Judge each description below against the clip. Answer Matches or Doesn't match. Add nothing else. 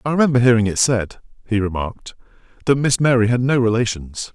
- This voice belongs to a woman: Doesn't match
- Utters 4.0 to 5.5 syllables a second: Doesn't match